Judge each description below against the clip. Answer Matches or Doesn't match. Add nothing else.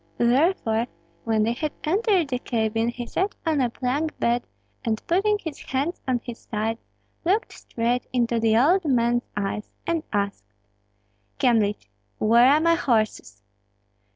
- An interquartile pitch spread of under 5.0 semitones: Doesn't match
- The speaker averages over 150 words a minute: Doesn't match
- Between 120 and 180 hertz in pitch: Doesn't match